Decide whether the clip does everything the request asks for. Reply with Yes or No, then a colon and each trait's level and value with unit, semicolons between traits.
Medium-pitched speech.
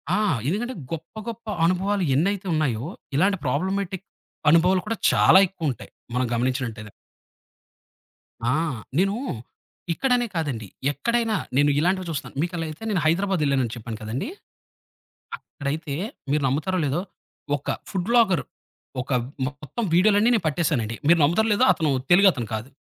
Yes: medium, 165 Hz